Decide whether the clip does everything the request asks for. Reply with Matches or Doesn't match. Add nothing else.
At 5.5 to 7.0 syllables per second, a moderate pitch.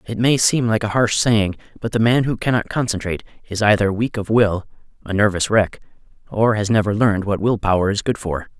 Doesn't match